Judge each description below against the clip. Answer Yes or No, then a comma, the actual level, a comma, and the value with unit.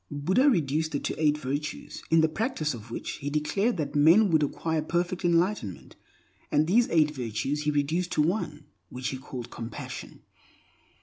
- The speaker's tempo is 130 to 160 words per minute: No, average, 170 wpm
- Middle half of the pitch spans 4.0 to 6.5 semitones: No, average, 3.2 semitones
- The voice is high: No, medium, 155 Hz